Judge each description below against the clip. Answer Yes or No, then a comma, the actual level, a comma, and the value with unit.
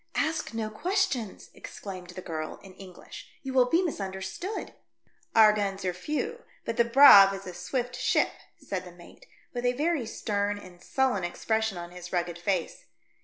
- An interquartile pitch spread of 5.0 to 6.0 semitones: Yes, wide, 5.6 semitones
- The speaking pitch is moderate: No, high, 205 Hz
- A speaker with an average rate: Yes, average, 170 wpm